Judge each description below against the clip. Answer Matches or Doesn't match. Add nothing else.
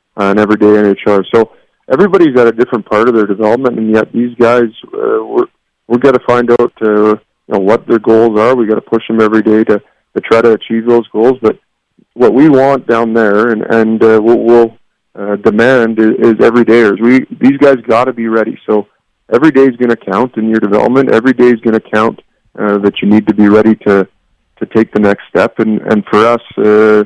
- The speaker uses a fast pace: Matches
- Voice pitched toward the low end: Matches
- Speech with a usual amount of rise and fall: Doesn't match